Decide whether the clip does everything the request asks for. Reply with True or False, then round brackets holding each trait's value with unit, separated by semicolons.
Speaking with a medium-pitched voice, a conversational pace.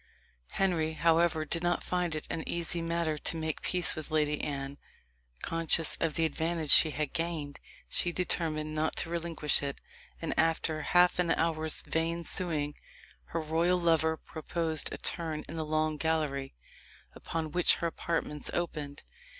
True (160 Hz; 160 wpm)